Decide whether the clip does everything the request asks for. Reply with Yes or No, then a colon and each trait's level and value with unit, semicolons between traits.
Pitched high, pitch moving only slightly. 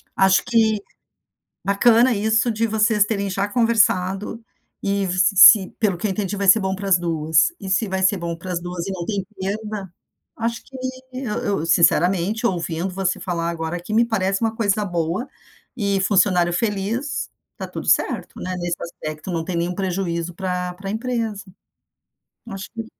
No: high, 195 Hz; average, 3.4 semitones